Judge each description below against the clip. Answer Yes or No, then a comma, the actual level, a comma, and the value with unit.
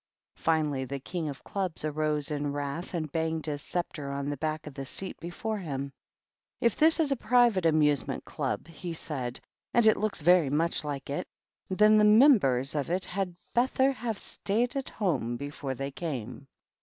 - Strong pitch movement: Yes, wide, 5.9 semitones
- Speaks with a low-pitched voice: No, medium, 160 Hz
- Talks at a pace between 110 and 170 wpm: No, average, 180 wpm